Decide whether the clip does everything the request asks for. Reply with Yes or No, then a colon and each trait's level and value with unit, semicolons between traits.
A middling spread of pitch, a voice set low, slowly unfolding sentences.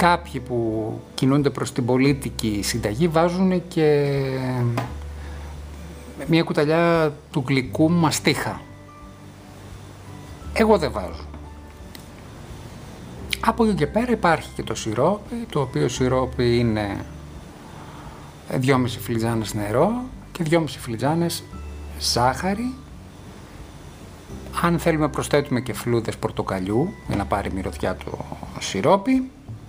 No: wide, 8.2 semitones; low, 125 Hz; slow, 100 wpm